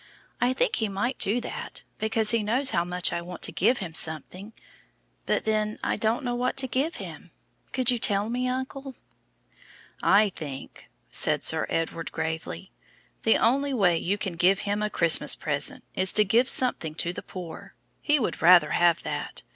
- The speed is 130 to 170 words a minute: No, average, 180 wpm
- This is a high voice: Yes, high, 210 Hz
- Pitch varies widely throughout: Yes, wide, 6.1 semitones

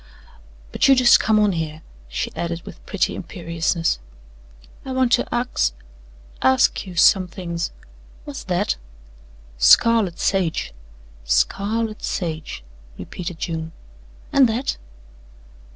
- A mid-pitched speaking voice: Yes, medium, 180 Hz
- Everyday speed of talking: No, slow, 110 wpm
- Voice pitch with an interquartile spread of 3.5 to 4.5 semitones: No, wide, 5.4 semitones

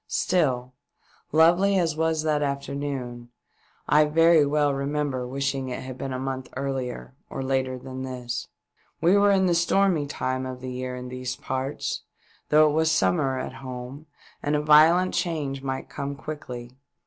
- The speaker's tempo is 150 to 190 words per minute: Yes, average, 160 wpm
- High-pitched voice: No, medium, 140 Hz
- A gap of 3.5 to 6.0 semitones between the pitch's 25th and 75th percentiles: No, average, 3.1 semitones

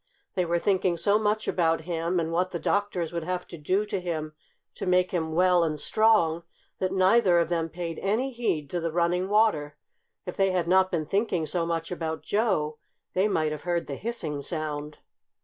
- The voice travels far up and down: No, average, 2.8 semitones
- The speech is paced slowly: No, average, 200 wpm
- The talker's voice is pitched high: No, medium, 175 Hz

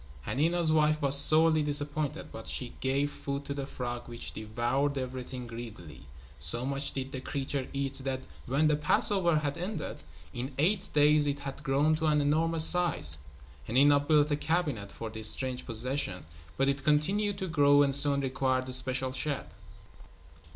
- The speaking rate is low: No, average, 165 wpm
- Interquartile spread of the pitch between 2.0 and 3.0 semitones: Yes, average, 2.7 semitones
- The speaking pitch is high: No, medium, 140 Hz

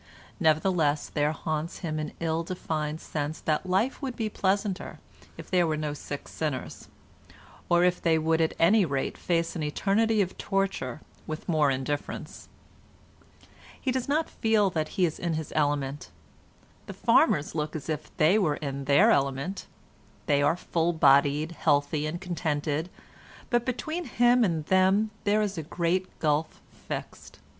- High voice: No, medium, 160 Hz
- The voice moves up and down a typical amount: Yes, average, 4.1 semitones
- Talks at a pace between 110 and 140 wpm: No, average, 155 wpm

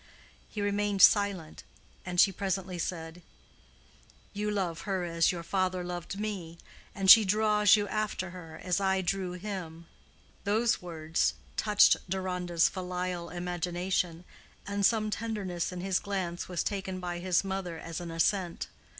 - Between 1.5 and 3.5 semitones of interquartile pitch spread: Yes, narrow, 2.4 semitones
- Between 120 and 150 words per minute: Yes, average, 140 wpm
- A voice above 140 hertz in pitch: Yes, medium, 185 Hz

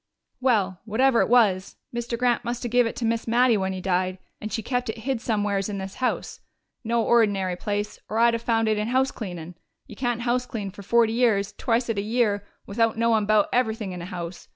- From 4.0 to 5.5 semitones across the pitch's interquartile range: No, average, 3.0 semitones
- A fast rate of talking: Yes, fast, 215 wpm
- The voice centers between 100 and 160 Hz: No, high, 225 Hz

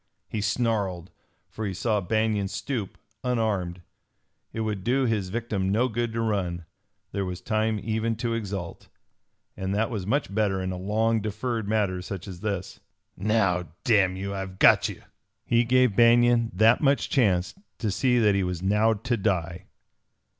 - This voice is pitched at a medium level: No, low, 105 Hz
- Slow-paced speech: No, average, 165 wpm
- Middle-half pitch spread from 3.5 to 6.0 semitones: No, average, 3.1 semitones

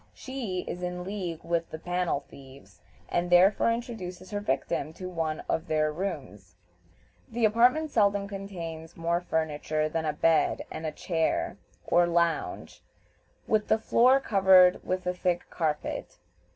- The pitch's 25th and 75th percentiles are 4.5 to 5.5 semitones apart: No, average, 3.7 semitones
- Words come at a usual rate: Yes, average, 145 wpm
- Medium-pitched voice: Yes, medium, 175 Hz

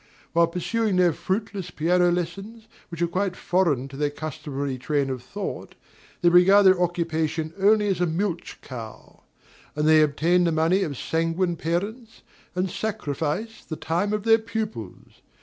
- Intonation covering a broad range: No, average, 3.8 semitones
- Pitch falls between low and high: Yes, medium, 175 Hz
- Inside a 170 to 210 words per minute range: No, average, 155 wpm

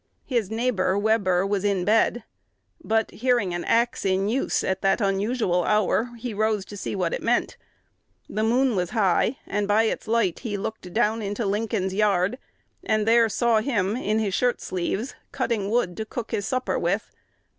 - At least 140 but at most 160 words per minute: No, average, 175 wpm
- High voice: Yes, high, 215 Hz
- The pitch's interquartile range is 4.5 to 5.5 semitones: No, average, 3.0 semitones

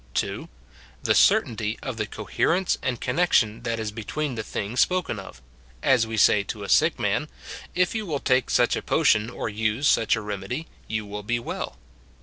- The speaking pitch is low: Yes, low, 115 Hz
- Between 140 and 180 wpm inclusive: No, average, 190 wpm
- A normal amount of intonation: Yes, average, 3.8 semitones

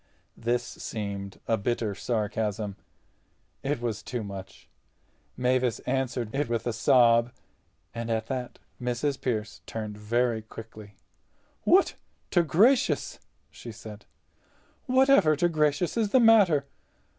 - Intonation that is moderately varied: Yes, average, 4.9 semitones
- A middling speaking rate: No, slow, 115 wpm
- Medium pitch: No, low, 120 Hz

